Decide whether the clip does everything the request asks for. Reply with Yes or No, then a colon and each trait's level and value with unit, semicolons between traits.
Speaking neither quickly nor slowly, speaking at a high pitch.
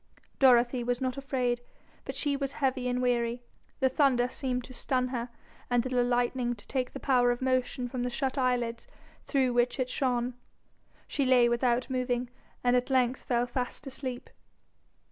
Yes: average, 170 wpm; very high, 250 Hz